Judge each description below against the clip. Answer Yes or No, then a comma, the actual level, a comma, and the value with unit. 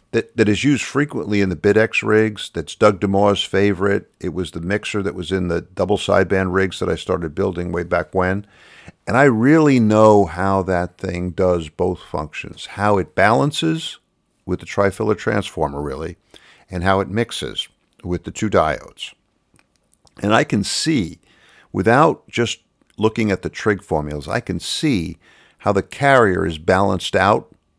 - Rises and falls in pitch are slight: No, average, 3.2 semitones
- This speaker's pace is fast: No, average, 165 wpm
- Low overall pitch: Yes, low, 100 Hz